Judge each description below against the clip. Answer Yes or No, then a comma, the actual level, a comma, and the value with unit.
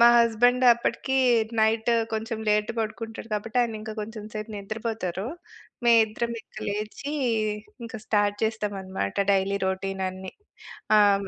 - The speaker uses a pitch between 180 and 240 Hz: Yes, high, 215 Hz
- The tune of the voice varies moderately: No, narrow, 2.1 semitones